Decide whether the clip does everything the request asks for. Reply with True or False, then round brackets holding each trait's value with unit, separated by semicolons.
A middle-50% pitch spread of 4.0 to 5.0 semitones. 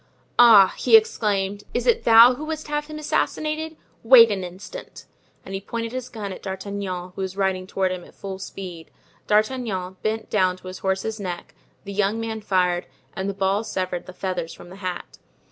False (3.5 semitones)